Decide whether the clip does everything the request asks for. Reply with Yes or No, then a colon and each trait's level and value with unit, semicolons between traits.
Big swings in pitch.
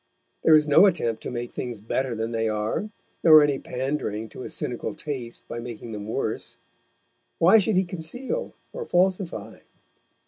Yes: wide, 7.0 semitones